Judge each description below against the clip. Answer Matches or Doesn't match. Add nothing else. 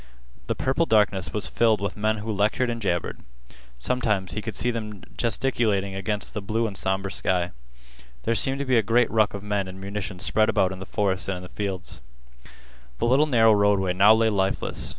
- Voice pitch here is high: Doesn't match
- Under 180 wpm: Doesn't match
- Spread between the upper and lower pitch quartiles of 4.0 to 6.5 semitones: Doesn't match